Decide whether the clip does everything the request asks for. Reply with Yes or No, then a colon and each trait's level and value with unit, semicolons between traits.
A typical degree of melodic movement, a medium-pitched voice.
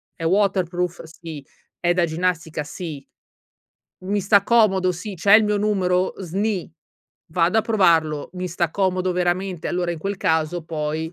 Yes: average, 3.0 semitones; medium, 180 Hz